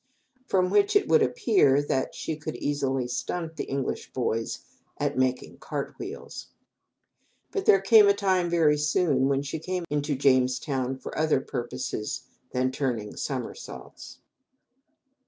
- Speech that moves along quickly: No, slow, 135 wpm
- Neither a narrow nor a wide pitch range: No, wide, 5.8 semitones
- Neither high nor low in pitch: Yes, medium, 145 Hz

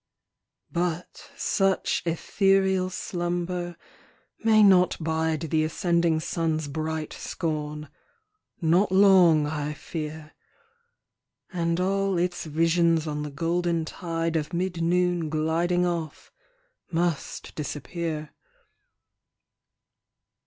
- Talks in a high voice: No, medium, 170 Hz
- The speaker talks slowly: Yes, slow, 90 wpm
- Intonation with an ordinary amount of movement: No, narrow, 2.1 semitones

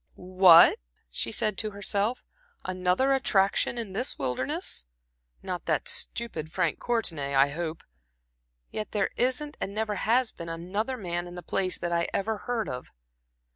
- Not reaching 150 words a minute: No, average, 155 wpm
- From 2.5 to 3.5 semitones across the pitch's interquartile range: No, average, 5.2 semitones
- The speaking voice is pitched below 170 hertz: No, medium, 185 Hz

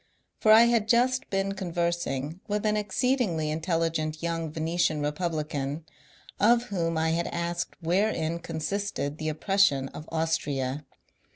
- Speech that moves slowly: Yes, slow, 125 wpm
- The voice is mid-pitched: Yes, medium, 165 Hz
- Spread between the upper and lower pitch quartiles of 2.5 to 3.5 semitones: No, average, 4.1 semitones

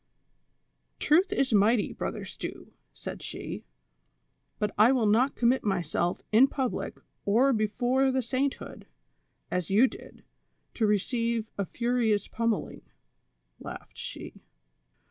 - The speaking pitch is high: Yes, high, 230 Hz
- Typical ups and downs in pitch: Yes, average, 3.7 semitones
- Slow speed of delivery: Yes, slow, 115 wpm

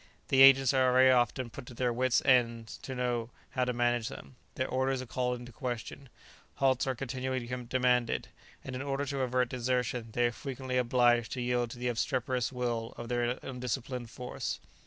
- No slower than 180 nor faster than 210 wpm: Yes, average, 185 wpm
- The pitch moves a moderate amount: No, narrow, 1.3 semitones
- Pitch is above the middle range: No, low, 125 Hz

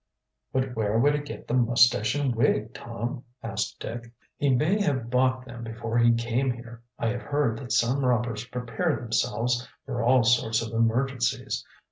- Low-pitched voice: Yes, low, 120 Hz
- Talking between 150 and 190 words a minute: Yes, average, 170 wpm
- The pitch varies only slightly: Yes, narrow, 2.0 semitones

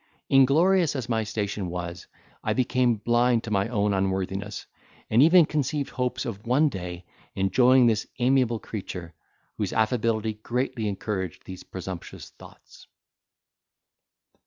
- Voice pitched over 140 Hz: No, low, 110 Hz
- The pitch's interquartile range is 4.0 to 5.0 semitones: Yes, average, 4.6 semitones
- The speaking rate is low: Yes, slow, 125 wpm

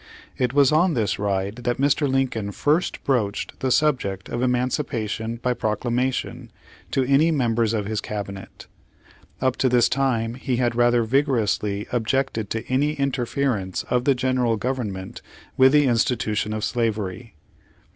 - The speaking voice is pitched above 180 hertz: No, low, 120 Hz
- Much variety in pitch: No, average, 3.4 semitones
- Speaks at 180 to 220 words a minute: No, average, 145 wpm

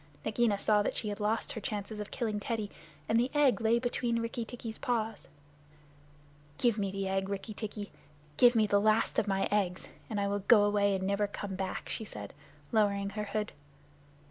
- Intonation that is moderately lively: No, narrow, 2.1 semitones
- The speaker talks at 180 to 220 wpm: Yes, average, 195 wpm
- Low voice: No, high, 210 Hz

